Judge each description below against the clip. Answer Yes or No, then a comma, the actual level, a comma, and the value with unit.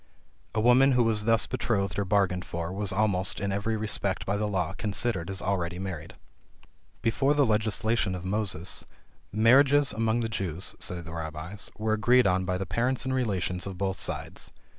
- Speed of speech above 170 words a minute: Yes, average, 180 wpm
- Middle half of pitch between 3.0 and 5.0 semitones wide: Yes, average, 3.6 semitones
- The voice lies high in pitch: No, low, 100 Hz